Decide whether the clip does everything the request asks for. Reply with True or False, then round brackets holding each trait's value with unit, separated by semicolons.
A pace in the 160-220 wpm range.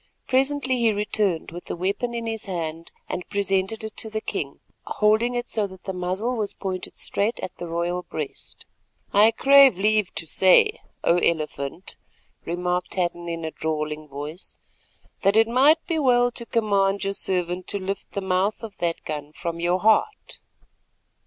True (170 wpm)